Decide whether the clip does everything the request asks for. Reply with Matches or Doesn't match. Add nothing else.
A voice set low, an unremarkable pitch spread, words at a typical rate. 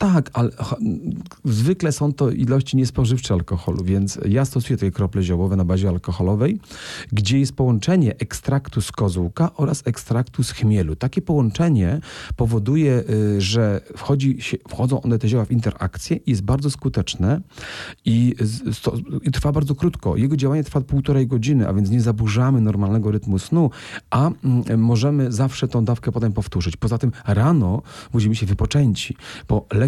Matches